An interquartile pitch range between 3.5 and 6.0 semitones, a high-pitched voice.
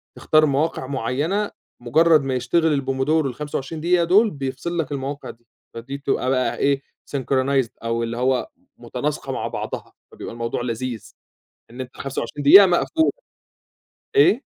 No: average, 3.9 semitones; medium, 140 Hz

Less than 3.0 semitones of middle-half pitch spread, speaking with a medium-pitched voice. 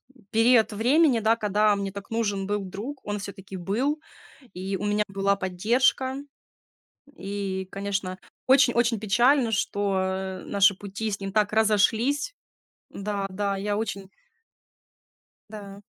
No: narrow, 2.4 semitones; high, 205 Hz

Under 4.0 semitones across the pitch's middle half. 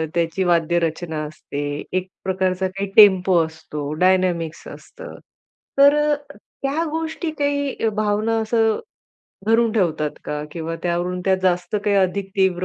No: average, 4.5 semitones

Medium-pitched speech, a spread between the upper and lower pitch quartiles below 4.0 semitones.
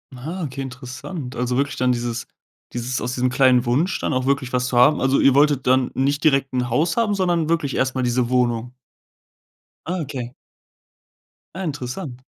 No: low, 130 Hz; average, 2.7 semitones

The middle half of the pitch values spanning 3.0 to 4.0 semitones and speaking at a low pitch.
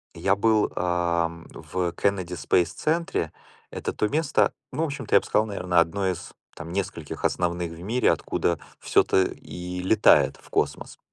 Yes: average, 3.4 semitones; very low, 90 Hz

